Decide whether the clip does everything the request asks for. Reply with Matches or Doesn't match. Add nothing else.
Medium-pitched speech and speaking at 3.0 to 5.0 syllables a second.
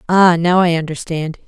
Matches